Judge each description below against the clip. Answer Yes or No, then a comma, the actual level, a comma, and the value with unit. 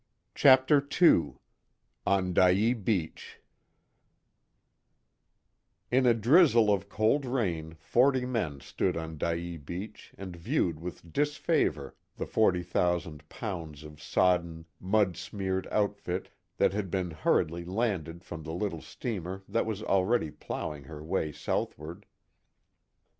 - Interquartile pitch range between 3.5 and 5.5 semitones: Yes, average, 4.8 semitones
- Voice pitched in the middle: No, very low, 90 Hz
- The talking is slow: Yes, slow, 120 wpm